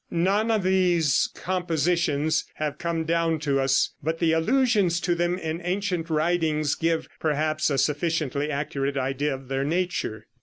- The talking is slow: No, average, 150 wpm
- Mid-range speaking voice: Yes, medium, 160 Hz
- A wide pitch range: No, average, 3.2 semitones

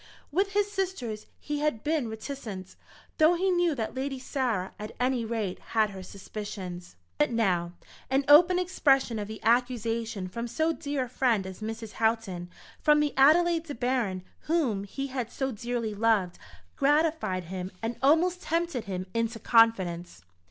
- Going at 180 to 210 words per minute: No, average, 160 wpm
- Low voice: No, high, 235 Hz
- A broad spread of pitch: Yes, wide, 6.0 semitones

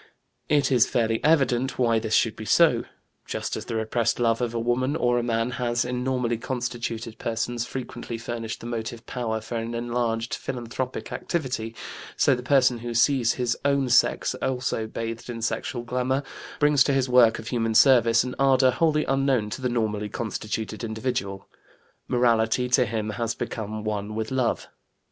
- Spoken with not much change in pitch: Yes, narrow, 2.0 semitones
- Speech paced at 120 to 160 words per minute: No, average, 170 wpm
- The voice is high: No, low, 120 Hz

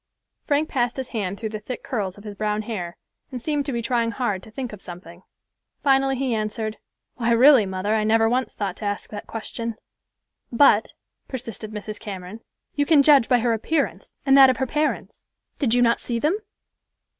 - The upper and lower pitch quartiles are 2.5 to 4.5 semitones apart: Yes, average, 3.9 semitones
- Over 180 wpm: Yes, average, 195 wpm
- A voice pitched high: Yes, high, 230 Hz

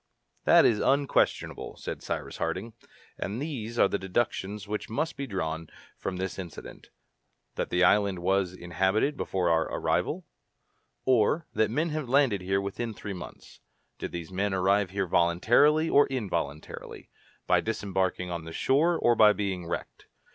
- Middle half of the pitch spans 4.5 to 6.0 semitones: Yes, average, 4.8 semitones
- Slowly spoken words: No, average, 155 wpm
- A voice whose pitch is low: Yes, low, 100 Hz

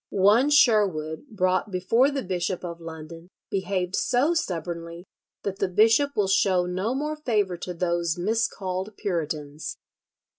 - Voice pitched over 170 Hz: Yes, medium, 185 Hz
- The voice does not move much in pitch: No, average, 4.2 semitones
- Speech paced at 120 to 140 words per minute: Yes, slow, 135 wpm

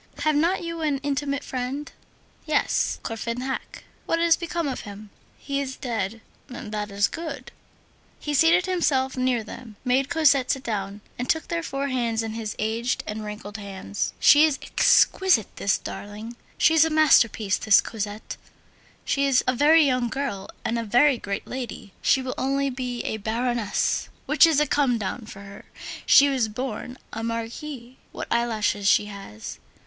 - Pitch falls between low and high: No, very high, 250 Hz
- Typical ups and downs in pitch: Yes, average, 4.7 semitones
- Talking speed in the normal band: Yes, average, 165 wpm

